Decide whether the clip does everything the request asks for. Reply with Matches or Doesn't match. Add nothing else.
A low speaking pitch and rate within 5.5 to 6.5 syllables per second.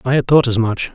Matches